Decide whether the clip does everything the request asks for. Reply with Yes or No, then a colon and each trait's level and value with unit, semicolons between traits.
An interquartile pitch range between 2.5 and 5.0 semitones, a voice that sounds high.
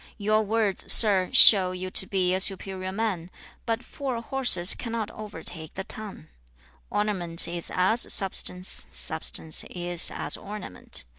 Yes: average, 3.1 semitones; high, 195 Hz